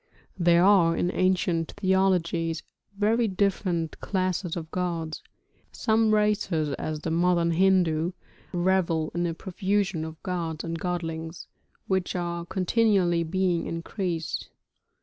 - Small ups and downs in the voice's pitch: Yes, narrow, 2.3 semitones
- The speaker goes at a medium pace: No, slow, 115 wpm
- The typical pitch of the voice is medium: Yes, medium, 175 Hz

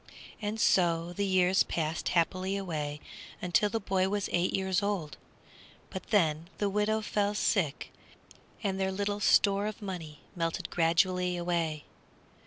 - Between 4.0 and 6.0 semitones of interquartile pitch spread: No, average, 3.2 semitones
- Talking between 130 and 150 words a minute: Yes, average, 140 wpm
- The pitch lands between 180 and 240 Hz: Yes, medium, 185 Hz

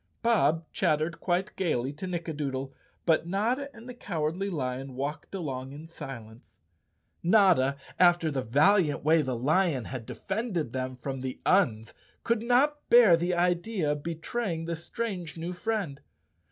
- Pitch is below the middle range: No, medium, 165 Hz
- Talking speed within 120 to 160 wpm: Yes, average, 145 wpm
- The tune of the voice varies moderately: No, wide, 5.8 semitones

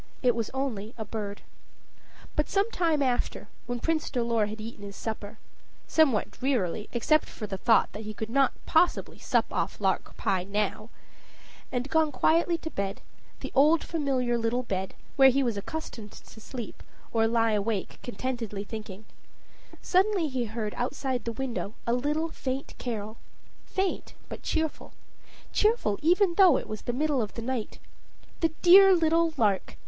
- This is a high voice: Yes, high, 245 Hz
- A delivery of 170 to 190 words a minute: No, average, 160 wpm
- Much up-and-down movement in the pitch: Yes, wide, 6.2 semitones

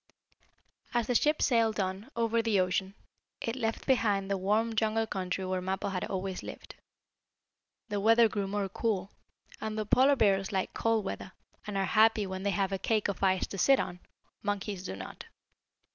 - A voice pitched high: Yes, high, 205 Hz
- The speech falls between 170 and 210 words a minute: Yes, average, 180 wpm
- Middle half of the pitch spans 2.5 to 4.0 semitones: Yes, average, 2.8 semitones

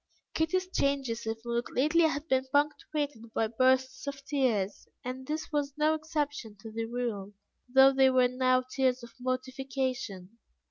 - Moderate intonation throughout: Yes, average, 3.3 semitones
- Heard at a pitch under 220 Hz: No, very high, 260 Hz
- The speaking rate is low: No, average, 150 wpm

